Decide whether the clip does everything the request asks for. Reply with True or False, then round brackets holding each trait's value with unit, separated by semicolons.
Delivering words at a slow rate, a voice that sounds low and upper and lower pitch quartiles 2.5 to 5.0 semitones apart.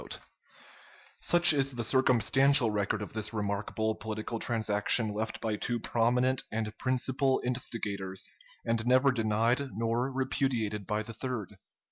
True (130 wpm; 115 Hz; 3.1 semitones)